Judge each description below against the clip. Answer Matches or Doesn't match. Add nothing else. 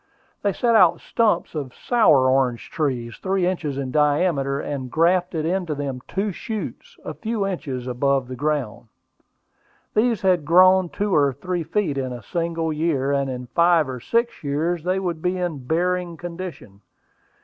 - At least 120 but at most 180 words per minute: Matches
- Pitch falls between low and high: Matches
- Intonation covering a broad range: Doesn't match